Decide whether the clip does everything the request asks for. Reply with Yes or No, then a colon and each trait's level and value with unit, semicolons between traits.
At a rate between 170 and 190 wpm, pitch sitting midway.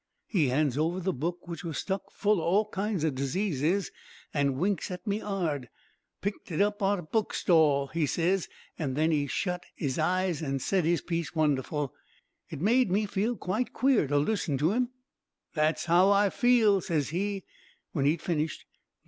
Yes: average, 175 wpm; medium, 170 Hz